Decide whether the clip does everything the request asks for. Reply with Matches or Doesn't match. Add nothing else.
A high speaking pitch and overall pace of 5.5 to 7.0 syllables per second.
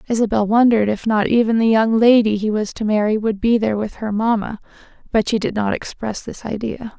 Matches